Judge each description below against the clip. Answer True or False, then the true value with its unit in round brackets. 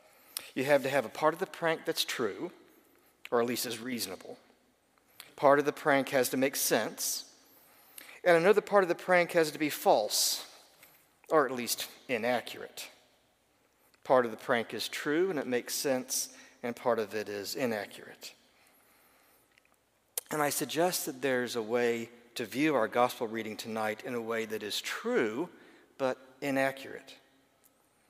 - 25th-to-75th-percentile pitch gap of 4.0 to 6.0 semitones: True (4.4 semitones)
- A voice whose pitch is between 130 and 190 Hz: True (135 Hz)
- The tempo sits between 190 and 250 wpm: False (160 wpm)